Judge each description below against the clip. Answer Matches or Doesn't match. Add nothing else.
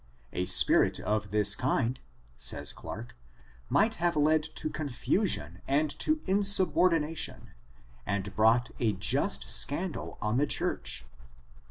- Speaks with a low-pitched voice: Matches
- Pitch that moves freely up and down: Matches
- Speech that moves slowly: Matches